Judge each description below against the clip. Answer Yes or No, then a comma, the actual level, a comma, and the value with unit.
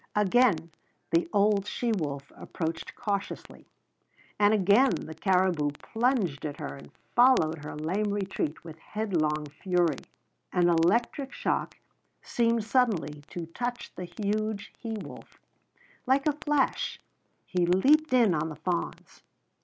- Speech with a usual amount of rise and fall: No, wide, 5.9 semitones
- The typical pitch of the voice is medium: No, high, 195 Hz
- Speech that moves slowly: Yes, slow, 130 wpm